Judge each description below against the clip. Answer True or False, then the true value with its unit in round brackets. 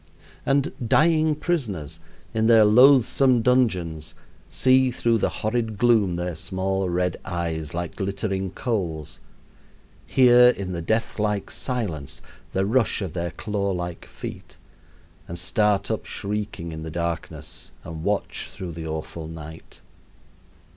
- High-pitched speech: False (100 Hz)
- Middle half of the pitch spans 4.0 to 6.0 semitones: True (5.4 semitones)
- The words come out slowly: True (130 wpm)